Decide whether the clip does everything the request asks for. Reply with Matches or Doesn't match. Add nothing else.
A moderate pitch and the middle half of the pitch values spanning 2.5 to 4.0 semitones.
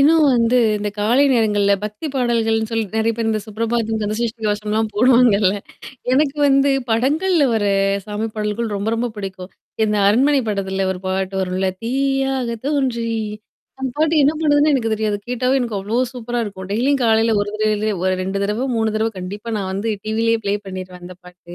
Doesn't match